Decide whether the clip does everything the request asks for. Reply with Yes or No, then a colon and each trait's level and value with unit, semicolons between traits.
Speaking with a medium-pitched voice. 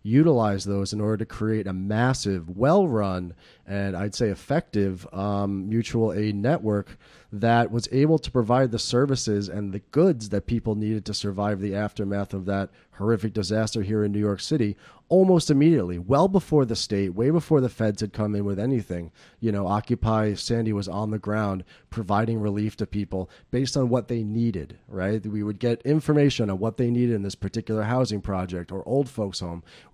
No: low, 110 Hz